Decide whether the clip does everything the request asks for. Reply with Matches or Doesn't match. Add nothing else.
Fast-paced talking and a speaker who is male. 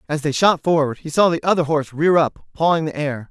Matches